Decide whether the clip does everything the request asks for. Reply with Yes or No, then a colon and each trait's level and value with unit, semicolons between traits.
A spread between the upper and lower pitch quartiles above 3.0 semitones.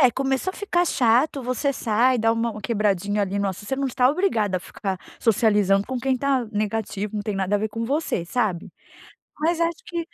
Yes: average, 4.6 semitones